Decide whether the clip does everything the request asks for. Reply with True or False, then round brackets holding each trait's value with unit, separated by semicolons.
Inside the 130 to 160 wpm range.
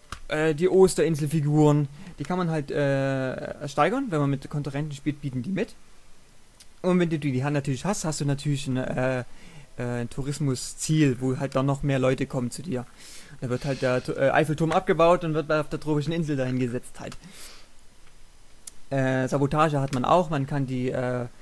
False (175 wpm)